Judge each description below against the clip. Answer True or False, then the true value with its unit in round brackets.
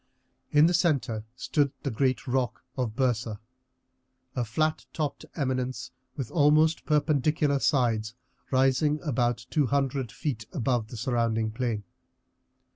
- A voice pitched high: False (130 Hz)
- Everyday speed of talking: False (120 wpm)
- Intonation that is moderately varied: True (3.8 semitones)